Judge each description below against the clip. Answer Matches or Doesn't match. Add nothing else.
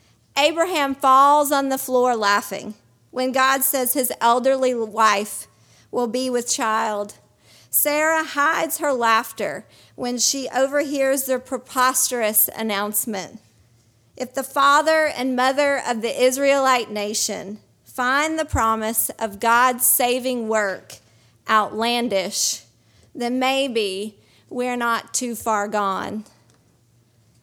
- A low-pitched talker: Doesn't match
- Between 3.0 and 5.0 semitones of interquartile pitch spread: Matches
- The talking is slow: Matches